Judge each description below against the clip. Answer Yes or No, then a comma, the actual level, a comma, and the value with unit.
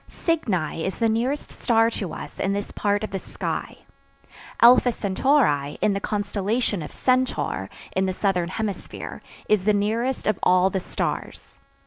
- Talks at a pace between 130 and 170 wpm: Yes, average, 155 wpm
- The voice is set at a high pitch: Yes, high, 205 Hz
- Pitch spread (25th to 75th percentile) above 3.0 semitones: Yes, average, 3.6 semitones